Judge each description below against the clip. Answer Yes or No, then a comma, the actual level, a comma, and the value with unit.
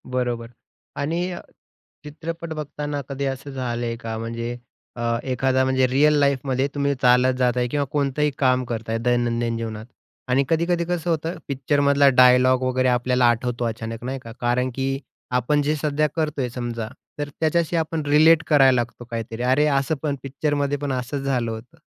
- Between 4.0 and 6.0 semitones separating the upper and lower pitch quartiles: No, average, 3.2 semitones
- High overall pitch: No, low, 130 Hz